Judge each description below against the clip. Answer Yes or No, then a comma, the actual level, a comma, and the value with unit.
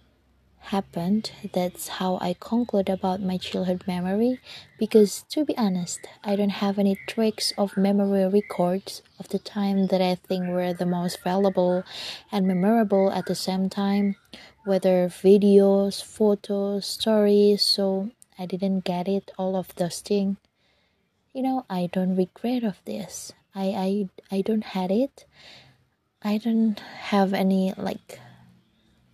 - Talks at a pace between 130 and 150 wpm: Yes, fast, 140 wpm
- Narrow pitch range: Yes, narrow, 1.6 semitones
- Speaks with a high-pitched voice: Yes, high, 195 Hz